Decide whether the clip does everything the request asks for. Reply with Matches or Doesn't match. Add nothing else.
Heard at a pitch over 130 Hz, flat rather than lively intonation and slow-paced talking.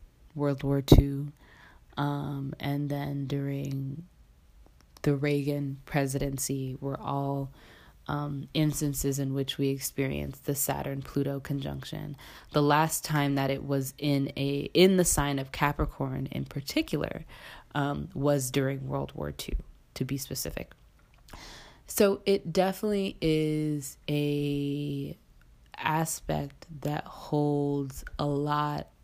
Matches